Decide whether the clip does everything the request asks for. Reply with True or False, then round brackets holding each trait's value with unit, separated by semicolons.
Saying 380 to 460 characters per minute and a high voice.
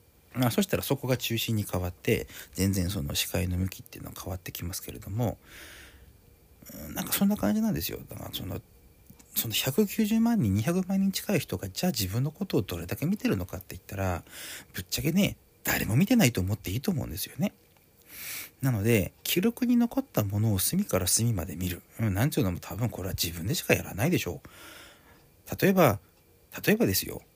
False (390 characters per minute; 105 Hz)